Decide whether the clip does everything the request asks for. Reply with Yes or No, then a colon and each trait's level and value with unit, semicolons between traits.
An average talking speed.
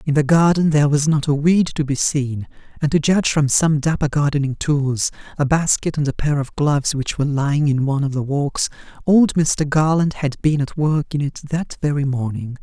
No: fast, 220 wpm